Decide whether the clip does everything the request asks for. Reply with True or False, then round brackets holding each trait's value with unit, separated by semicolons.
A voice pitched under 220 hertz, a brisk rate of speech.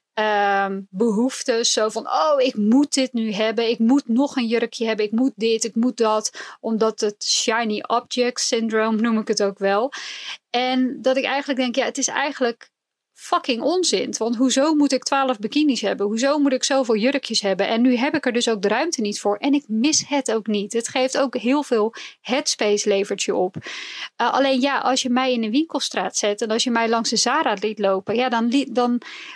False (240 Hz; 215 wpm)